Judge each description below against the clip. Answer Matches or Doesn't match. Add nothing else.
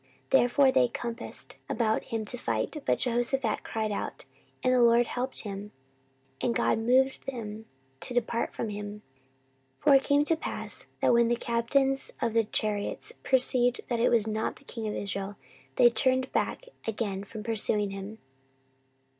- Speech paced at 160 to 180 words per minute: Matches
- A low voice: Doesn't match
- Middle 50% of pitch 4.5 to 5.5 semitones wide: Doesn't match